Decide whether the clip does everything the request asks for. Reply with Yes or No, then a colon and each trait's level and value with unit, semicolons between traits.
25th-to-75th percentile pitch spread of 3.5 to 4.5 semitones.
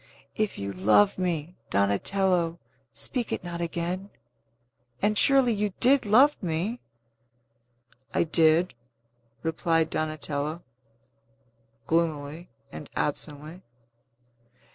Yes: average, 4.2 semitones